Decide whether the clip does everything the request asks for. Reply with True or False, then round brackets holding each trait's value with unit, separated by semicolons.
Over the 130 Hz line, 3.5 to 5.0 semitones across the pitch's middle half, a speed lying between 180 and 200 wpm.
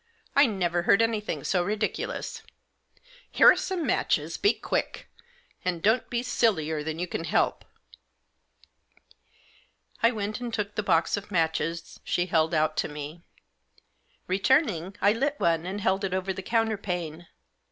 False (190 Hz; 4.7 semitones; 150 wpm)